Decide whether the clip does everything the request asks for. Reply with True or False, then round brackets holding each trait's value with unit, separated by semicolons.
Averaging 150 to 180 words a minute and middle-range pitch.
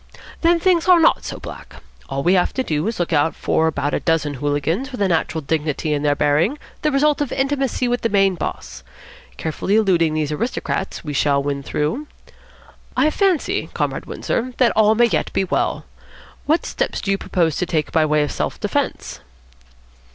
False (195 wpm; 180 Hz)